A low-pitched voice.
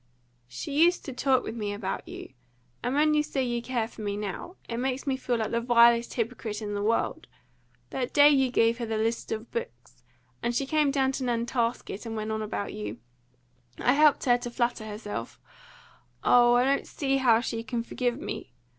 No: high, 240 Hz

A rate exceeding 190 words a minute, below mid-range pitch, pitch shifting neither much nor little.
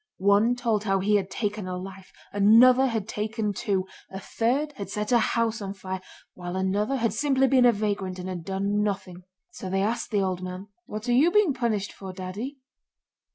No: average, 200 wpm; high, 205 Hz; average, 3.6 semitones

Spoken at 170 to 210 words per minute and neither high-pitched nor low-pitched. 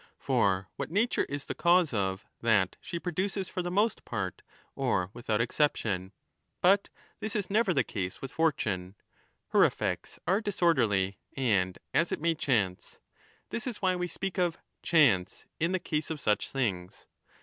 Yes: average, 180 wpm; medium, 145 Hz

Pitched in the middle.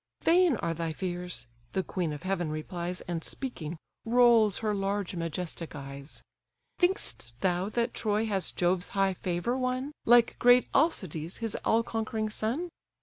No: high, 195 Hz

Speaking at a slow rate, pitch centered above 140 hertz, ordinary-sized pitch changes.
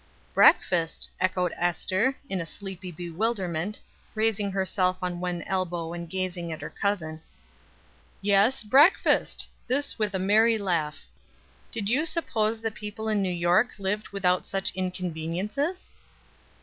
Yes: slow, 130 wpm; high, 190 Hz; average, 3.4 semitones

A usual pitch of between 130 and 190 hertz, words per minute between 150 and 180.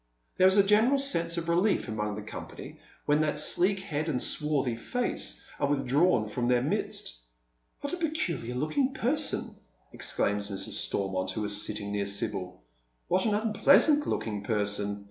Yes: medium, 140 Hz; average, 170 wpm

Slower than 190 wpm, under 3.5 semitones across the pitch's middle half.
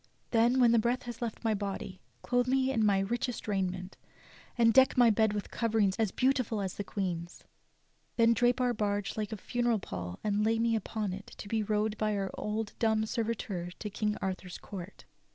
No: average, 195 wpm; average, 2.7 semitones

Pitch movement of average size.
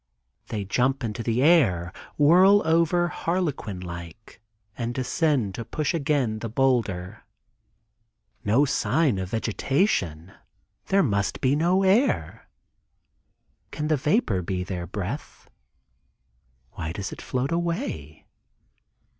No: wide, 8.4 semitones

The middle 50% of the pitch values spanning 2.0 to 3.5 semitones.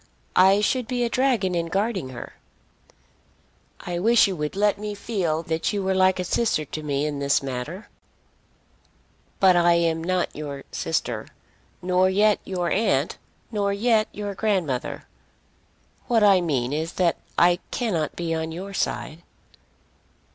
No: average, 4.3 semitones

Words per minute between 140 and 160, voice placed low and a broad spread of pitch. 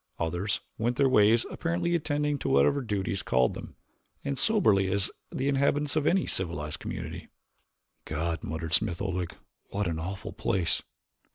Yes: average, 150 wpm; low, 105 Hz; wide, 8.8 semitones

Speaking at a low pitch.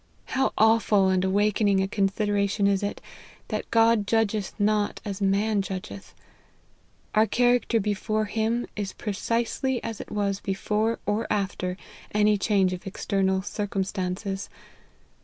No: high, 205 Hz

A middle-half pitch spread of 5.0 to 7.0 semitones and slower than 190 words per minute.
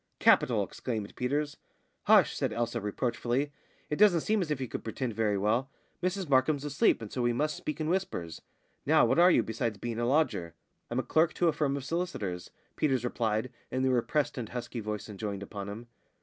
No: average, 5.3 semitones; average, 200 wpm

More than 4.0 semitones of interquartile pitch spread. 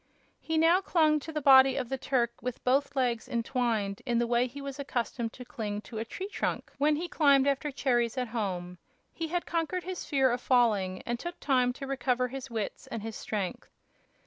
No: average, 3.4 semitones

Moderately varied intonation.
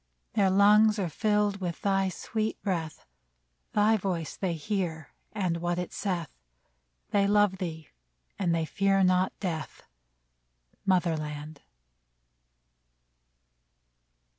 Yes: average, 3.4 semitones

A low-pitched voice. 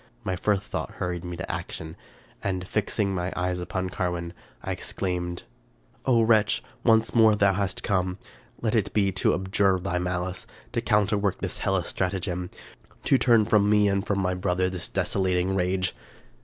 Yes: very low, 95 Hz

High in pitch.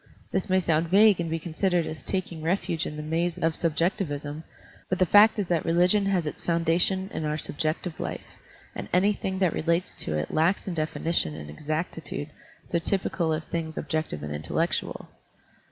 No: medium, 165 Hz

